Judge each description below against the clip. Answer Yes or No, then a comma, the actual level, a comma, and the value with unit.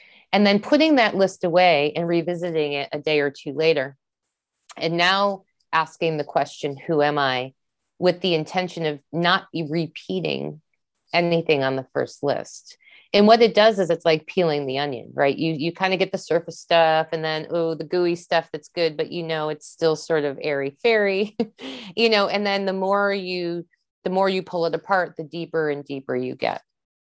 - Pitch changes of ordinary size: Yes, average, 3.7 semitones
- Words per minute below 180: No, average, 195 wpm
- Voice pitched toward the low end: No, medium, 165 Hz